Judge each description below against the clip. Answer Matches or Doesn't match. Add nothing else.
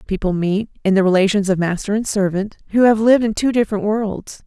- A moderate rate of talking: Doesn't match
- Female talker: Matches